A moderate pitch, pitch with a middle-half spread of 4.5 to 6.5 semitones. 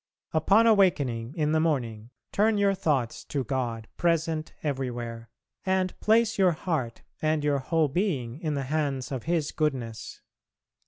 Yes: medium, 150 Hz; average, 5.3 semitones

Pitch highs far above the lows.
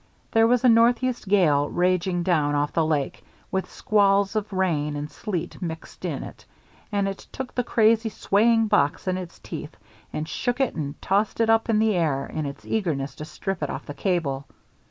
Yes: wide, 6.3 semitones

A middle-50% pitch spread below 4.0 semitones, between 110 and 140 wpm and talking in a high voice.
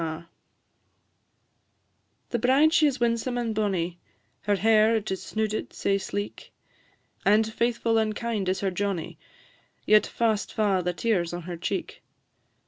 Yes: average, 3.1 semitones; slow, 135 wpm; high, 215 Hz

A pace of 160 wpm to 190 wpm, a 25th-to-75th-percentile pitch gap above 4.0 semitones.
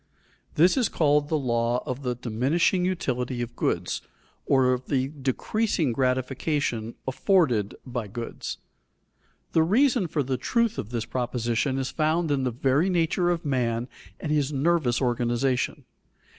No: average, 145 wpm; average, 4.7 semitones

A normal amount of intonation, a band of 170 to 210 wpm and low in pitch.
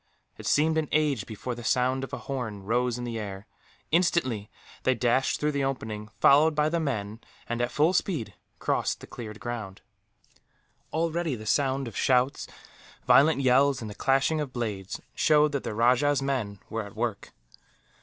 Yes: average, 4.3 semitones; average, 175 wpm; low, 130 Hz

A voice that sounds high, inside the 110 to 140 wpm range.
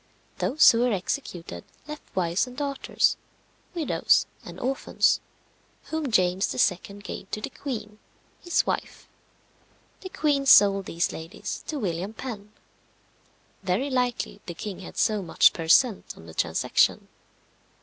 Yes: high, 210 Hz; slow, 135 wpm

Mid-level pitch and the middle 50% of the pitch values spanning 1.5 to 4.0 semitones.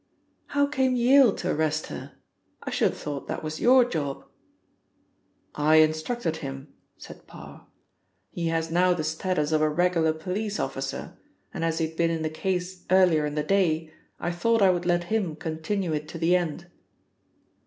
Yes: medium, 165 Hz; average, 3.0 semitones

